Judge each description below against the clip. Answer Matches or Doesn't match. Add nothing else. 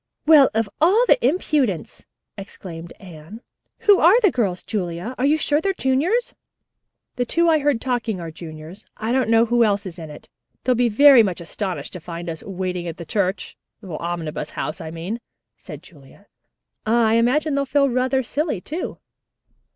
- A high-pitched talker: Matches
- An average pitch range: Doesn't match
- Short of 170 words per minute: Doesn't match